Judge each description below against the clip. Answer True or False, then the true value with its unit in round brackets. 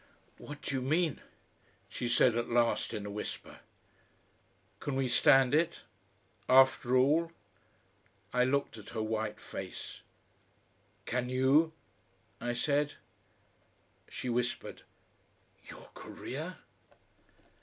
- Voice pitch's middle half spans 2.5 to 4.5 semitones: True (3.0 semitones)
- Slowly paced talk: True (105 wpm)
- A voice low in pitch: True (130 Hz)